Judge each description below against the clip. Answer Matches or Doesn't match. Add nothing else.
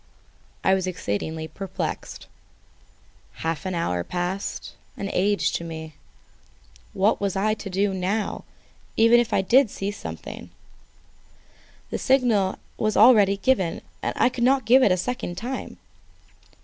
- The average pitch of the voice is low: Doesn't match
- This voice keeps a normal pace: Doesn't match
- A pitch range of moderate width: Matches